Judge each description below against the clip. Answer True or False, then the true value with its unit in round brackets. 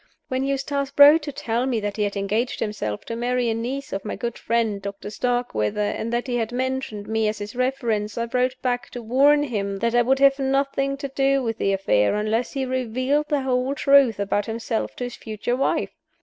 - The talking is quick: True (215 wpm)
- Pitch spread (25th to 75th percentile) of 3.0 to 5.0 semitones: True (3.8 semitones)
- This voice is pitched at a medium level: False (245 Hz)